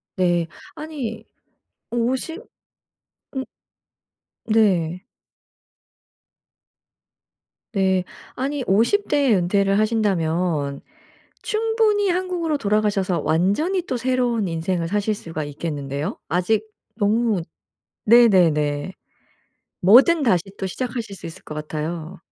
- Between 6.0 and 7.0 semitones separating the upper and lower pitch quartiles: Yes, wide, 6.5 semitones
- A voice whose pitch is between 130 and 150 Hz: No, high, 205 Hz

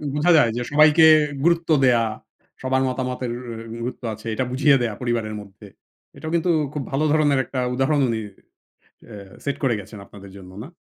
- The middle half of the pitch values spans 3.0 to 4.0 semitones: No, average, 4.8 semitones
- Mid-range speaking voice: No, low, 130 Hz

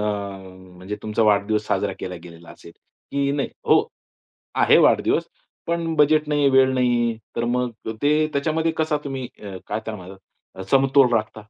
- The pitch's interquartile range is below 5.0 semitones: No, wide, 5.6 semitones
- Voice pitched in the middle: No, low, 120 Hz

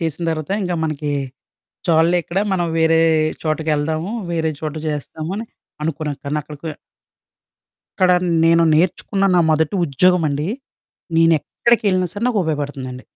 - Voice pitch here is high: No, medium, 160 Hz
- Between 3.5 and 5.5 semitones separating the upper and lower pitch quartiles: No, average, 2.8 semitones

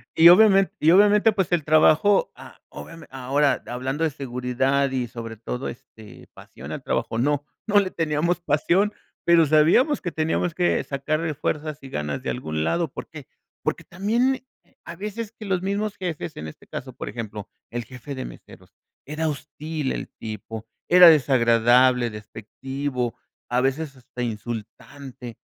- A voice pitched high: No, medium, 145 Hz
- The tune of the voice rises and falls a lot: Yes, wide, 5.8 semitones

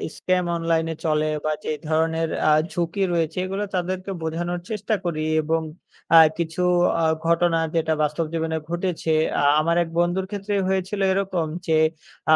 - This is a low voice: No, medium, 170 Hz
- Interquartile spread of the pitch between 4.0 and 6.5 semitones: No, narrow, 2.4 semitones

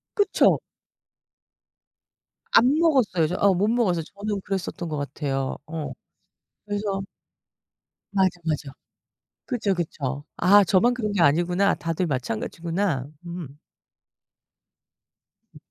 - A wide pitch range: No, average, 4.6 semitones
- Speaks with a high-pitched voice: No, medium, 180 Hz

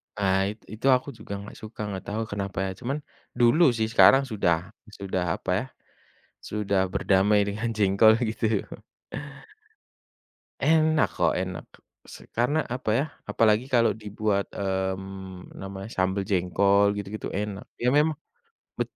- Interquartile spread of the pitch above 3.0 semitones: No, average, 2.7 semitones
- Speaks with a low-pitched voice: Yes, low, 100 Hz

